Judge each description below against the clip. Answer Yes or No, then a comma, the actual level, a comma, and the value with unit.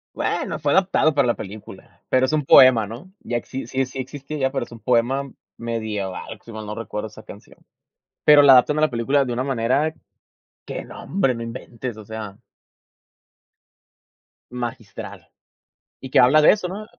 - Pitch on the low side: Yes, low, 125 Hz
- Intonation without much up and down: No, average, 3.5 semitones